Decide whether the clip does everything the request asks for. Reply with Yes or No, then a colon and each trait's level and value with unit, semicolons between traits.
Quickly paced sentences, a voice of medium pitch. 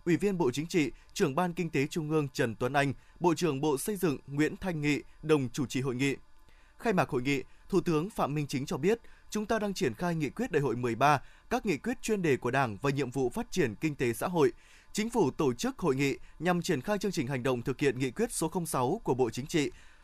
Yes: fast, 260 wpm; medium, 155 Hz